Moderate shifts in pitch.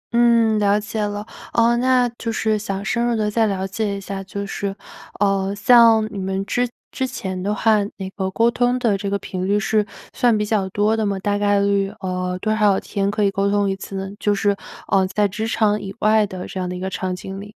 No: narrow, 2.1 semitones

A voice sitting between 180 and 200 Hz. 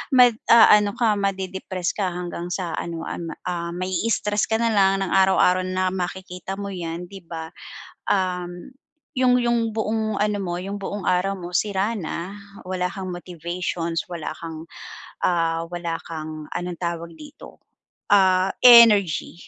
Yes: medium, 185 Hz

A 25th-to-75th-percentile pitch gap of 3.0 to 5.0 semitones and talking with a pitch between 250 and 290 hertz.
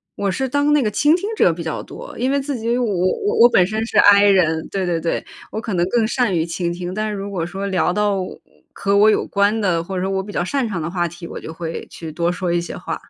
No: average, 4.2 semitones; high, 195 Hz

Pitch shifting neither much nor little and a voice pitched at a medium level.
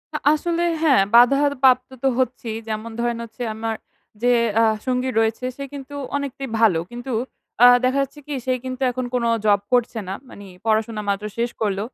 No: average, 3.0 semitones; high, 245 Hz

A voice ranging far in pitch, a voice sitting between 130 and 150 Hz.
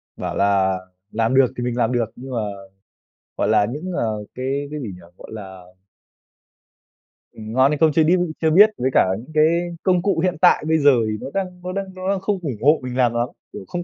Yes: wide, 7.2 semitones; low, 135 Hz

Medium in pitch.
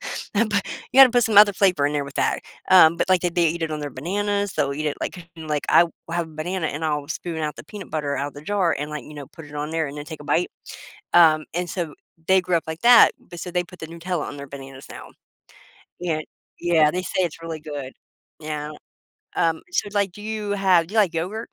Yes: medium, 165 Hz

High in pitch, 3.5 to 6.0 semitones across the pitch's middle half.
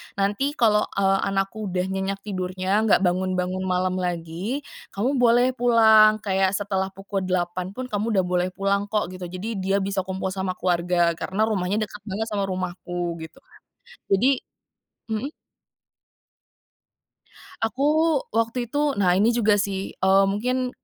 No: high, 195 Hz; average, 2.9 semitones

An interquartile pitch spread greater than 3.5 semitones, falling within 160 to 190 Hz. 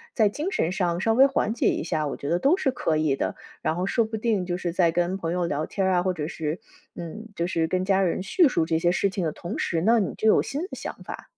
Yes: average, 4.7 semitones; medium, 185 Hz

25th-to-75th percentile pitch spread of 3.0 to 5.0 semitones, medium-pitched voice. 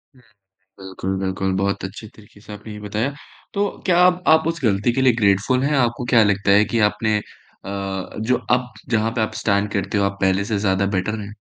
No: average, 3.6 semitones; low, 105 Hz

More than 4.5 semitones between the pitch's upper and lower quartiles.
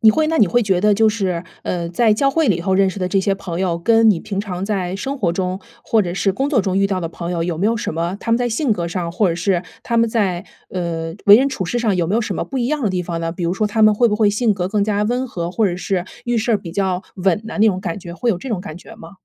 No: average, 3.9 semitones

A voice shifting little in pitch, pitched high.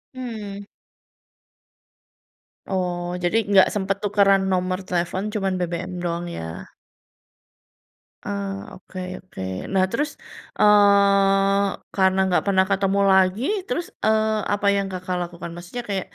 Yes: narrow, 1.7 semitones; high, 195 Hz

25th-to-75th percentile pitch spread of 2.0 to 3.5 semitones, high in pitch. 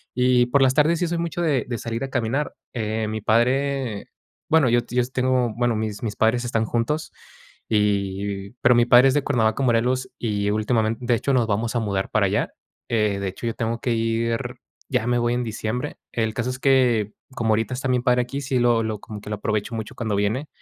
No: narrow, 2.6 semitones; low, 120 Hz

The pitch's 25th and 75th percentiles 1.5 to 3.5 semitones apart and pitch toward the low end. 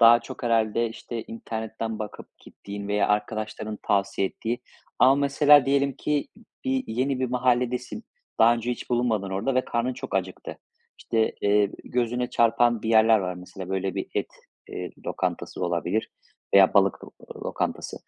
Yes: average, 3.0 semitones; low, 115 Hz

